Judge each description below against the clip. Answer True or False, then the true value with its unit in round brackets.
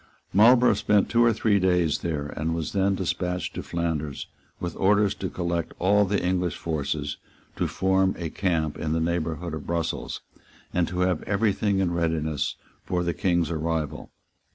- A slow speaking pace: False (170 wpm)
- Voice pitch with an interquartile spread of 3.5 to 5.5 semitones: False (3.0 semitones)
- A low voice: True (90 Hz)